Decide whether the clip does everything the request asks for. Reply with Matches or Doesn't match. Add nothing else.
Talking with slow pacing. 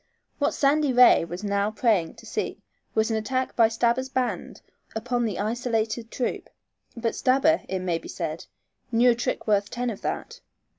Doesn't match